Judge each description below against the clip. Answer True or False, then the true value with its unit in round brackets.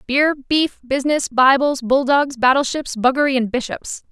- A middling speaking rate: False (130 wpm)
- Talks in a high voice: True (270 Hz)